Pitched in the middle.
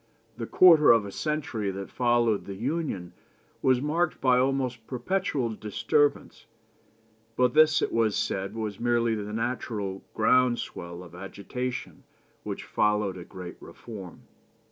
No: low, 115 Hz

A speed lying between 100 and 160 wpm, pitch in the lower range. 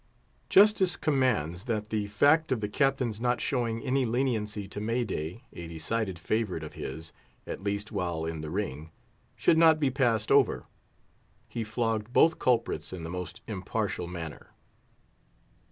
Yes: average, 145 wpm; low, 110 Hz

